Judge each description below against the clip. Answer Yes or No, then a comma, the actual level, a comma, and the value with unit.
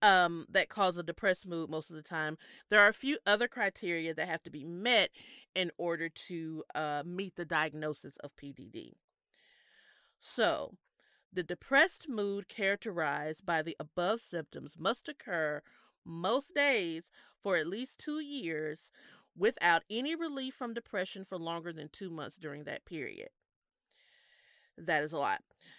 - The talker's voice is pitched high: No, medium, 175 Hz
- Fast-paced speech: No, average, 150 wpm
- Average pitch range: No, wide, 5.7 semitones